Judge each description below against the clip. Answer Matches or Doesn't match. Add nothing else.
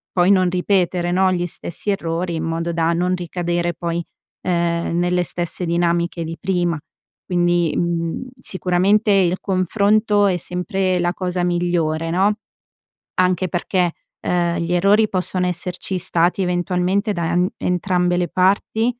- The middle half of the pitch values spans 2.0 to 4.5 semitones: Doesn't match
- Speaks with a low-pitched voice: Doesn't match